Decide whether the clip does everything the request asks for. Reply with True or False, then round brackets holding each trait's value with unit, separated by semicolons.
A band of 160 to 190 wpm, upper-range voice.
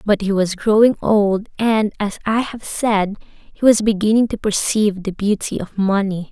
True (180 wpm; 205 Hz)